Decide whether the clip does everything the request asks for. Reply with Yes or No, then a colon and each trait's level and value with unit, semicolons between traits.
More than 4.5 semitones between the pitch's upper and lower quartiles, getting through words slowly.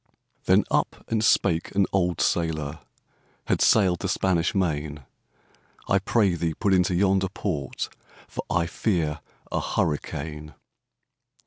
No: average, 3.8 semitones; slow, 125 wpm